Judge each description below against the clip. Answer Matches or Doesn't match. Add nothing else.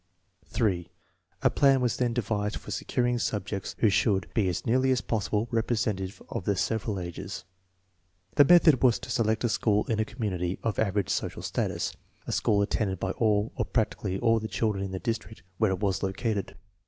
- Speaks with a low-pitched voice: Matches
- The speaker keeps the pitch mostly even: Doesn't match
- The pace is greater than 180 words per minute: Matches